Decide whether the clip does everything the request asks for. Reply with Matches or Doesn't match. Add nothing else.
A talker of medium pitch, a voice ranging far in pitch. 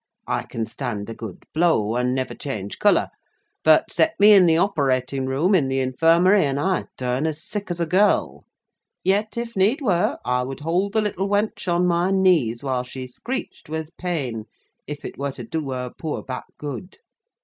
Matches